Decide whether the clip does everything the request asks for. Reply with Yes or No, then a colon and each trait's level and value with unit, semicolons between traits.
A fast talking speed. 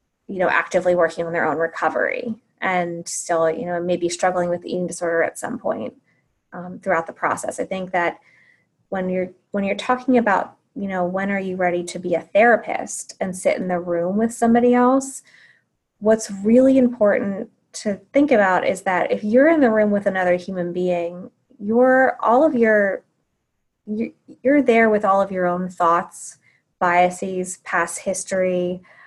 No: average, 175 wpm